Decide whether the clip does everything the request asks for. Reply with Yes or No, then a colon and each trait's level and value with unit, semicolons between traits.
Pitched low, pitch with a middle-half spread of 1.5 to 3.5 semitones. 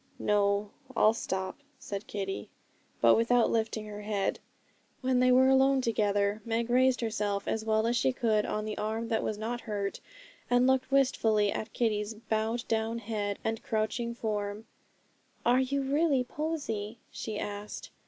No: high, 220 Hz; average, 2.8 semitones